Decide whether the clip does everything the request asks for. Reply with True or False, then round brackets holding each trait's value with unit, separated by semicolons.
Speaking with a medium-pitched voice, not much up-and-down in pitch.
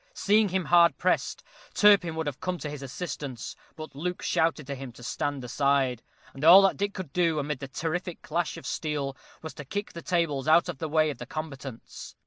False (155 Hz; 4.0 semitones)